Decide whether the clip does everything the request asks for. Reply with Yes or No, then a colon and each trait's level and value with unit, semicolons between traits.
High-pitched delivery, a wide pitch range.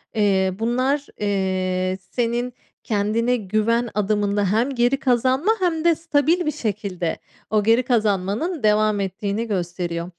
No: high, 215 Hz; average, 3.9 semitones